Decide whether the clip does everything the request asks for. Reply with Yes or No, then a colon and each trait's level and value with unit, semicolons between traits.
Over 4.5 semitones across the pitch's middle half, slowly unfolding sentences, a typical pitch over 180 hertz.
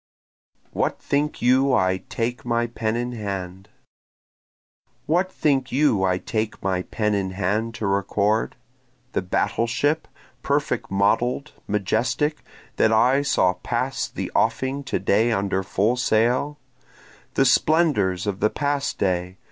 No: average, 5.0 semitones; slow, 130 wpm; low, 110 Hz